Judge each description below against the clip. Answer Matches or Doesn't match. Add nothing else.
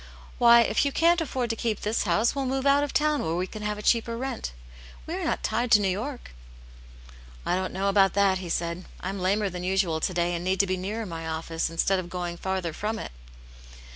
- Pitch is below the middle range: Doesn't match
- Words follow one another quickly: Matches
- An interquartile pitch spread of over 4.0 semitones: Matches